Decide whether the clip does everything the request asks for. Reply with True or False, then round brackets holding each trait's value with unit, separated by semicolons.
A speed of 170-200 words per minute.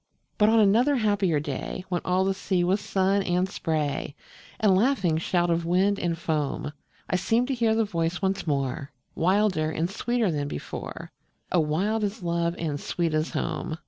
True (175 wpm)